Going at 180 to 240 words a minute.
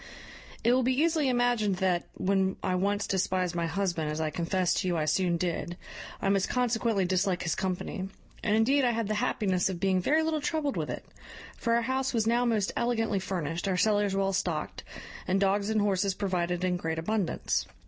Yes: average, 200 wpm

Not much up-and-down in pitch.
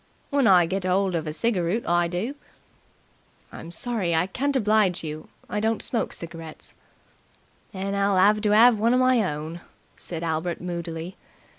No: average, 4.4 semitones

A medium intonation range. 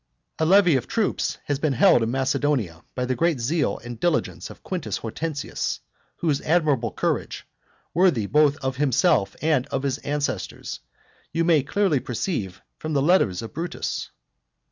Yes: average, 4.7 semitones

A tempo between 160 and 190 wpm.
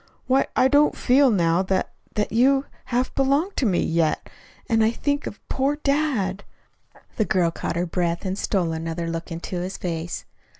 Yes: average, 175 wpm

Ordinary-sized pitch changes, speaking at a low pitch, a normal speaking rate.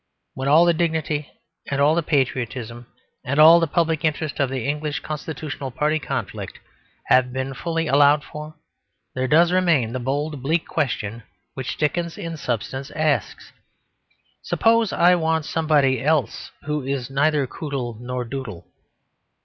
No: average, 3.2 semitones; medium, 145 Hz; average, 145 wpm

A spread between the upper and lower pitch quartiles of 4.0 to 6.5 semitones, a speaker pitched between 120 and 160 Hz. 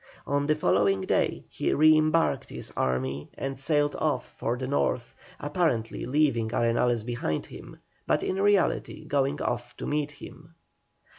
Yes: average, 4.5 semitones; medium, 140 Hz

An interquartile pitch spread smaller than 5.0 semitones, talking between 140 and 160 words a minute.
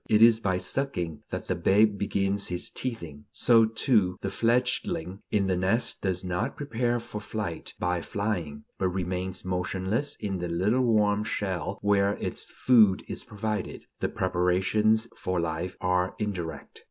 Yes: average, 3.4 semitones; average, 155 wpm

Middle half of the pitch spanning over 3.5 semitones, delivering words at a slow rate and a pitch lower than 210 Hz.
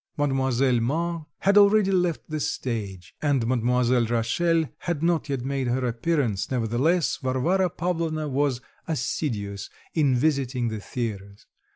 Yes: average, 5.3 semitones; slow, 130 wpm; low, 135 Hz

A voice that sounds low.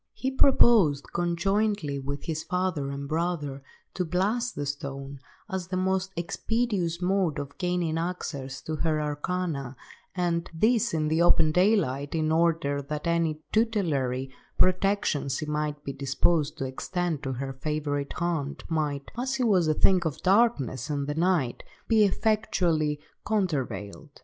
No: medium, 160 Hz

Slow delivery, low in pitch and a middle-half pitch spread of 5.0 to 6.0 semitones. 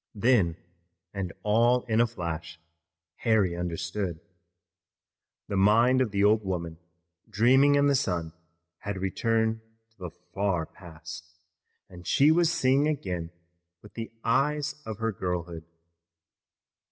Yes: slow, 125 wpm; low, 100 Hz; wide, 5.4 semitones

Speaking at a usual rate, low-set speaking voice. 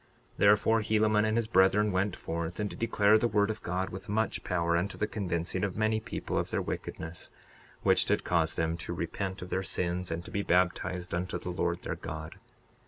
No: fast, 210 wpm; very low, 95 Hz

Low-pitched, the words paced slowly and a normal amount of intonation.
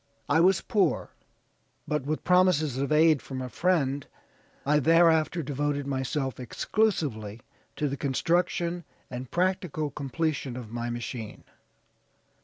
No: medium, 145 Hz; slow, 120 wpm; average, 4.2 semitones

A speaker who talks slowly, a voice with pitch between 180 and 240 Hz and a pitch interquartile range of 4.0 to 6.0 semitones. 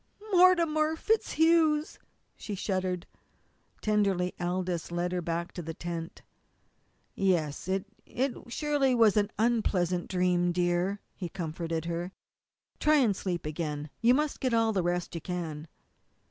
Yes: slow, 130 wpm; medium, 185 Hz; wide, 5.5 semitones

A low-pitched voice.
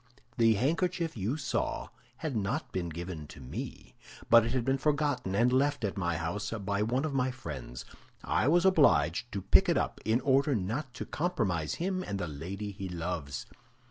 Yes: low, 110 Hz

